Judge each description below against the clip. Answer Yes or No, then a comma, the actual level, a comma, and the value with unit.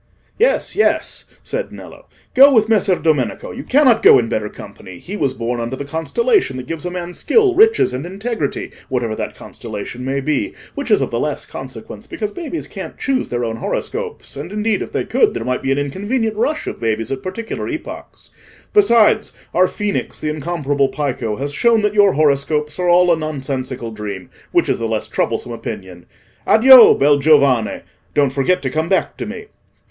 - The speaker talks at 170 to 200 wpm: Yes, average, 185 wpm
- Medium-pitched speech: Yes, medium, 155 Hz